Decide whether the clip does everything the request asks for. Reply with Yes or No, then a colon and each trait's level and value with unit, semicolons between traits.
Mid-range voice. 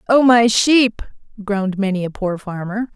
No: high, 210 Hz